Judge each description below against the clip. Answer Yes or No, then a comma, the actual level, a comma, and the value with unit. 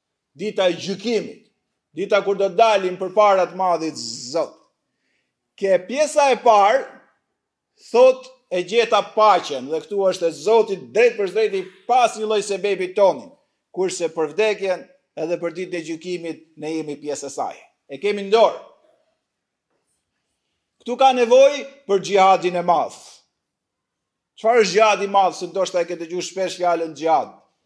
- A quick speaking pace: No, average, 145 wpm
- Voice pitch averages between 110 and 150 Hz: No, high, 195 Hz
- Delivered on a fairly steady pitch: No, average, 4.7 semitones